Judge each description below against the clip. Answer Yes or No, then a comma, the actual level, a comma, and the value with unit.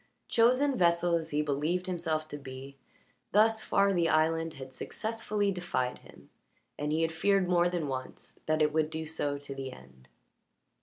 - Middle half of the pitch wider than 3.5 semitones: Yes, average, 4.1 semitones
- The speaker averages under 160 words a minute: No, average, 170 wpm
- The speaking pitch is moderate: Yes, medium, 160 Hz